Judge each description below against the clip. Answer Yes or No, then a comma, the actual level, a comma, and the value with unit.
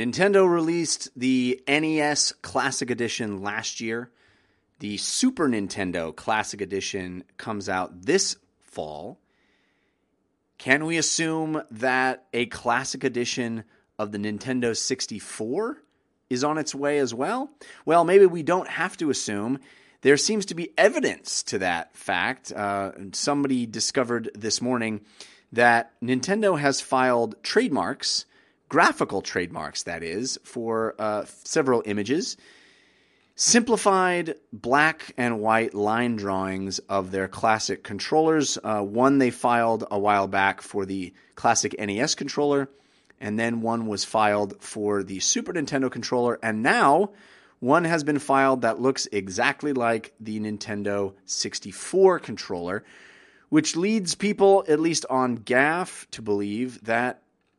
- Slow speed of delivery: Yes, slow, 130 wpm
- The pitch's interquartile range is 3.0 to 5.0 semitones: No, wide, 5.5 semitones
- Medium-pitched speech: No, low, 120 Hz